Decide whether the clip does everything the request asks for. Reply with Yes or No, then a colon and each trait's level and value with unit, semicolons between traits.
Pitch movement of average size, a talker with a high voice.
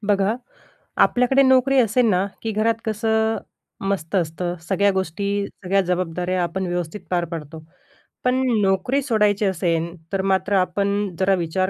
Yes: average, 3.3 semitones; high, 195 Hz